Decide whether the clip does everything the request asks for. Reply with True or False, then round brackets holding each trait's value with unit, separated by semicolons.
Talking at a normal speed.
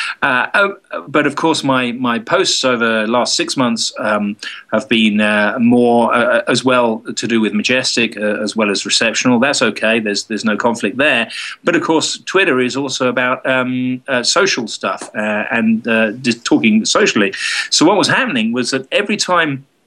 True (185 wpm)